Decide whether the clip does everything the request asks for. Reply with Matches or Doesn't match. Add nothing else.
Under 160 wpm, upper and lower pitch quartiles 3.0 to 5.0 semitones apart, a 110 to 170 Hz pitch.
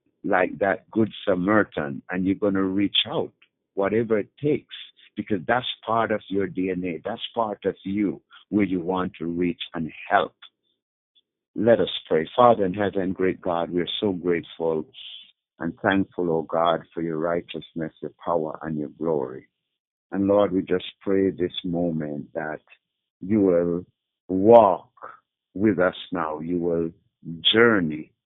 Doesn't match